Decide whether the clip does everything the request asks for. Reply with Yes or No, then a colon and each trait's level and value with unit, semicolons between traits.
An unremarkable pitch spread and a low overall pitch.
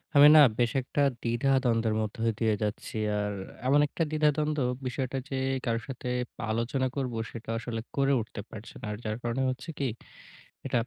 Yes: average, 3.2 semitones; low, 125 Hz